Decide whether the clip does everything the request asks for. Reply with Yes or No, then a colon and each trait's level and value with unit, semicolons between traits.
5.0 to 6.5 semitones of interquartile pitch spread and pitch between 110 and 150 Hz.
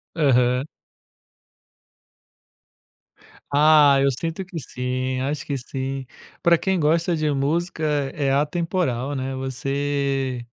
No: average, 3.1 semitones; medium, 140 Hz